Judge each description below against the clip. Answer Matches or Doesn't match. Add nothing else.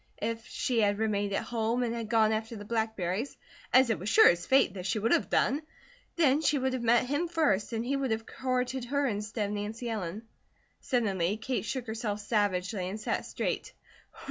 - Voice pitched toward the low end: Doesn't match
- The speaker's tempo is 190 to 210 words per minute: Matches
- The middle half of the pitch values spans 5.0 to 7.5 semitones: Doesn't match